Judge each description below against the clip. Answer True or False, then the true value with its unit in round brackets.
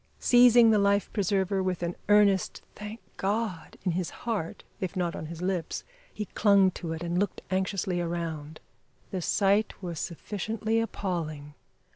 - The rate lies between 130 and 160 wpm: True (150 wpm)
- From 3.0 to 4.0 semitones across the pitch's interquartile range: True (3.3 semitones)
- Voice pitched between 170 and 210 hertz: True (190 Hz)